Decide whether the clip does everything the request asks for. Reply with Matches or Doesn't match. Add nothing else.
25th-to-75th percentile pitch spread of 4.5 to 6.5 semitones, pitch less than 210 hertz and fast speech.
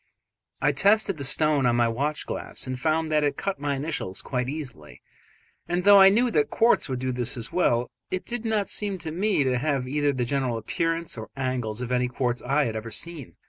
Matches